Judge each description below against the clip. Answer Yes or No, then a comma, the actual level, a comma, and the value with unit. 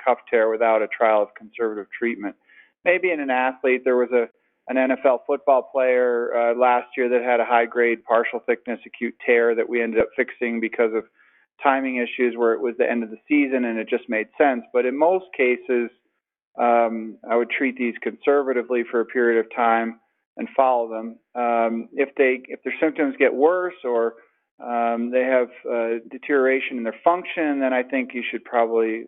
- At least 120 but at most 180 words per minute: No, average, 195 wpm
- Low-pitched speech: Yes, low, 120 Hz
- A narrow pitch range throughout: Yes, narrow, 2.0 semitones